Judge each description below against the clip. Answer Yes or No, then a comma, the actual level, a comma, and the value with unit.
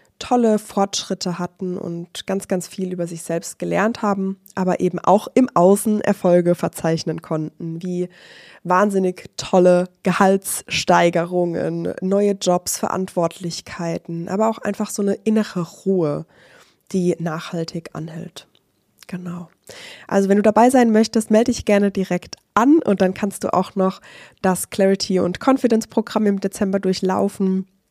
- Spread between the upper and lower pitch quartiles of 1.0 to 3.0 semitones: Yes, narrow, 2.6 semitones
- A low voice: No, high, 190 Hz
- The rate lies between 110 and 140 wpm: Yes, average, 135 wpm